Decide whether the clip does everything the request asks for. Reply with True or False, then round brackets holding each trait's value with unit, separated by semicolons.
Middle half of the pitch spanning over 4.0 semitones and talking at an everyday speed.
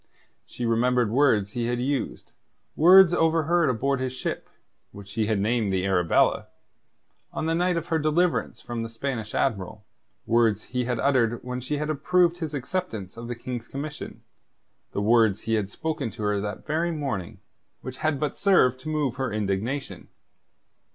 True (5.5 semitones; 170 wpm)